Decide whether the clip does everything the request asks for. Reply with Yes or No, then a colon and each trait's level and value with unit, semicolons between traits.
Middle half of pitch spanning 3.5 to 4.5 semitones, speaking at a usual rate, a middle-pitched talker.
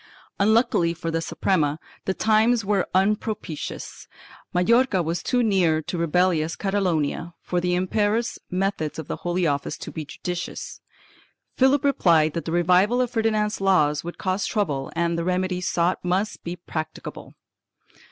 Yes: average, 3.8 semitones; average, 145 wpm; medium, 180 Hz